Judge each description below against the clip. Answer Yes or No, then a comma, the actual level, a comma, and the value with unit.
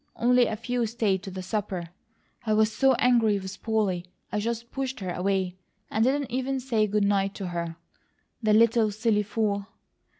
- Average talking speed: Yes, average, 175 wpm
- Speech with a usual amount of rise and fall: Yes, average, 3.1 semitones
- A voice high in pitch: Yes, high, 215 Hz